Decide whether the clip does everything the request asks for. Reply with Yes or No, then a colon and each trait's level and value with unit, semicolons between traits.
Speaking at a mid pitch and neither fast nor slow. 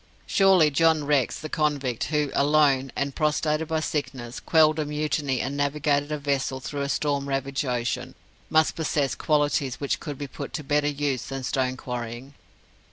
Yes: medium, 145 Hz; average, 165 wpm